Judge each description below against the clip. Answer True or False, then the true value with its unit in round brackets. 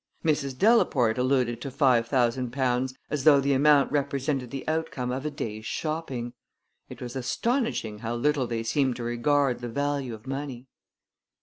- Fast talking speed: False (165 wpm)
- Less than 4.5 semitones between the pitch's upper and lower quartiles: True (3.0 semitones)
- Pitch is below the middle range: True (130 Hz)